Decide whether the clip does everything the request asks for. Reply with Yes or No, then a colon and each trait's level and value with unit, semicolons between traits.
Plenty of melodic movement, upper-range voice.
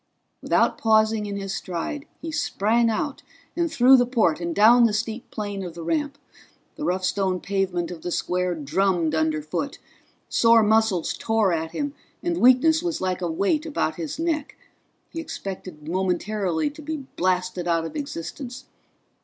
Yes: wide, 6.7 semitones; high, 205 Hz